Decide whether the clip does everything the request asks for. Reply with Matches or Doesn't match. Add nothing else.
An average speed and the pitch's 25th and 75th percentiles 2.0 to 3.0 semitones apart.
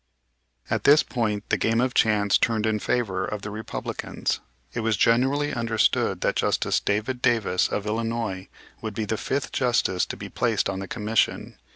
Matches